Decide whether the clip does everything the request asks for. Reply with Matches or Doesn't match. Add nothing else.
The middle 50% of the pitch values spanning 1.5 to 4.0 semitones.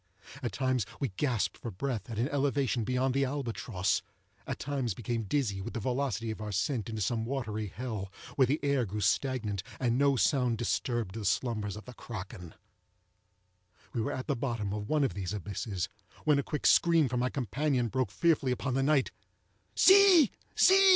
Doesn't match